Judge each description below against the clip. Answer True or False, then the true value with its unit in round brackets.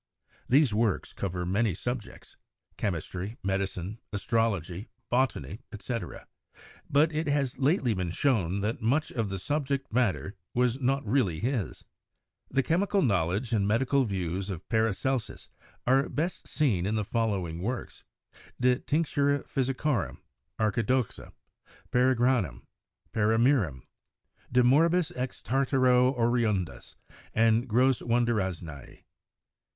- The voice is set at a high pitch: False (115 Hz)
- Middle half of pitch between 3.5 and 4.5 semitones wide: False (5.1 semitones)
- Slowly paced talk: True (115 wpm)